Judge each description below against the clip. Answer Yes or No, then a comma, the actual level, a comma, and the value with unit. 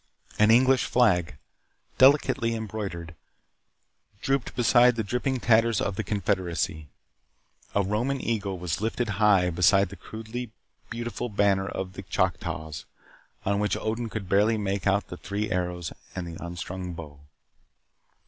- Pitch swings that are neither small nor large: Yes, average, 4.0 semitones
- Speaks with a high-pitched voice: No, low, 100 Hz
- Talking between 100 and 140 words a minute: Yes, slow, 135 wpm